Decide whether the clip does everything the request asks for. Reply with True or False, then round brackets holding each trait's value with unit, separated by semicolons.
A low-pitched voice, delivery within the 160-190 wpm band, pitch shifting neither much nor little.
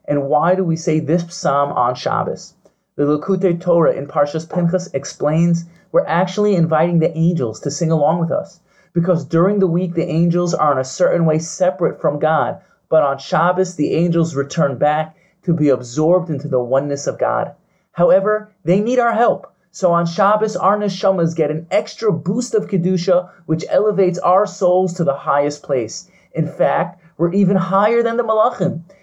False (175 Hz; 180 wpm; 3.1 semitones)